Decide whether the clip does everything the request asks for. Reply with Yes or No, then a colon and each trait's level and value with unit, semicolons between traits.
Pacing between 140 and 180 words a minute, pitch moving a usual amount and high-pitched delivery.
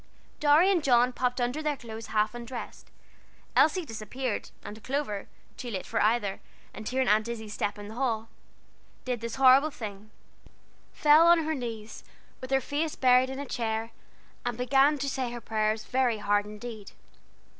Yes: average, 165 wpm; average, 3.6 semitones; high, 245 Hz